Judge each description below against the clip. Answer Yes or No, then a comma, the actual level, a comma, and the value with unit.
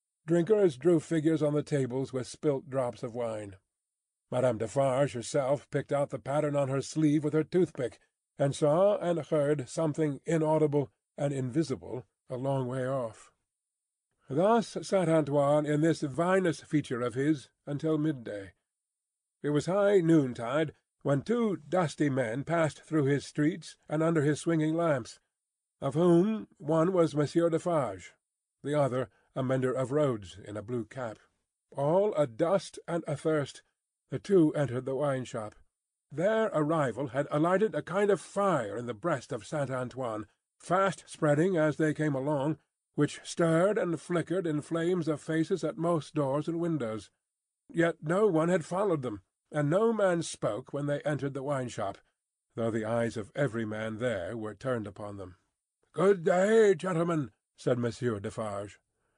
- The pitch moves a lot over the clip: No, average, 4.3 semitones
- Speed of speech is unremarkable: Yes, average, 160 wpm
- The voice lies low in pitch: No, medium, 150 Hz